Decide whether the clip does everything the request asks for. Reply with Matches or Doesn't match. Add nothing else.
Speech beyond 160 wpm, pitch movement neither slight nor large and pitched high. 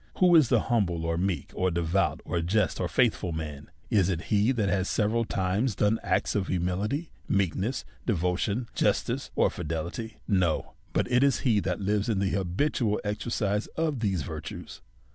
Doesn't match